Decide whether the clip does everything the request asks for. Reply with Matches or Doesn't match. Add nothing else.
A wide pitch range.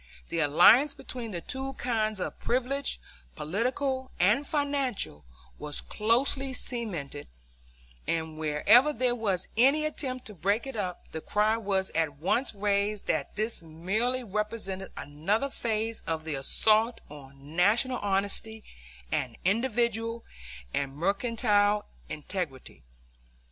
Matches